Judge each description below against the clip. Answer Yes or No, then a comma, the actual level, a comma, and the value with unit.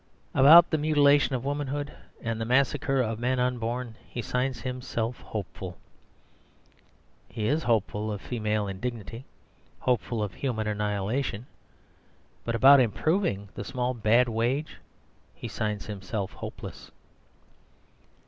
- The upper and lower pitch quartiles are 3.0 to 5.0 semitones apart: Yes, average, 3.9 semitones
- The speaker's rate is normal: No, slow, 120 wpm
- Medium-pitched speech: No, low, 120 Hz